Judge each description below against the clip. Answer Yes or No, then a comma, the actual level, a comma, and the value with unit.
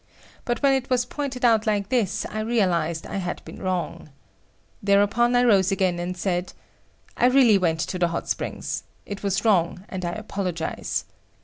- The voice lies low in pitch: No, high, 200 Hz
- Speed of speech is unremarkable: Yes, average, 180 wpm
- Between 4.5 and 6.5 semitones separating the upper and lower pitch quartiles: Yes, average, 4.9 semitones